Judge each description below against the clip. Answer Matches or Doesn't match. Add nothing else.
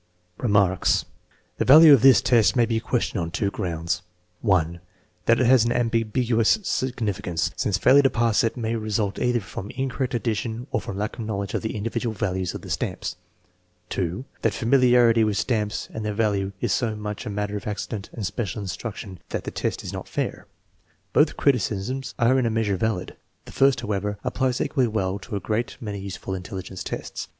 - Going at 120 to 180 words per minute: Doesn't match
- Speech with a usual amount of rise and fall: Matches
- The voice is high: Doesn't match